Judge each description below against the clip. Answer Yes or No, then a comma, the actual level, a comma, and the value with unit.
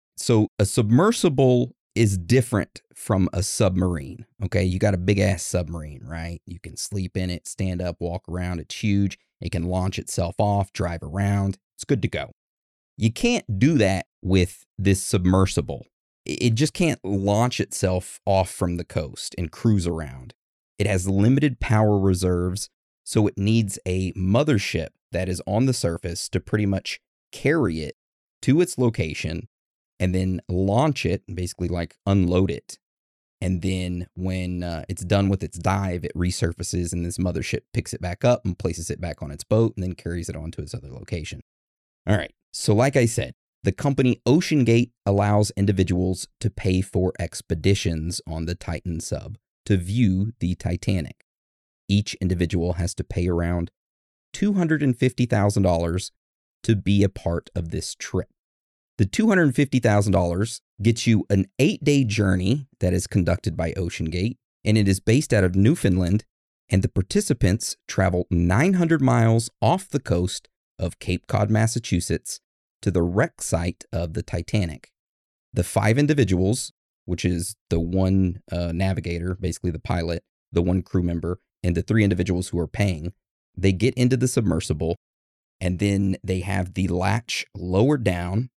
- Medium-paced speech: Yes, average, 160 wpm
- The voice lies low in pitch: Yes, very low, 95 Hz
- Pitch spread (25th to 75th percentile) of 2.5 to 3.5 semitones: No, average, 4.0 semitones